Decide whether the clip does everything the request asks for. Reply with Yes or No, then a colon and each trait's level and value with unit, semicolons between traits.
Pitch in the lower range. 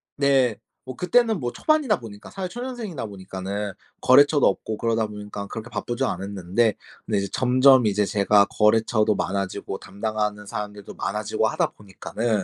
Yes: low, 110 Hz